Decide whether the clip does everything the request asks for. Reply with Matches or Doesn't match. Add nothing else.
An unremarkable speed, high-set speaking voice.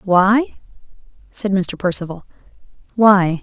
Doesn't match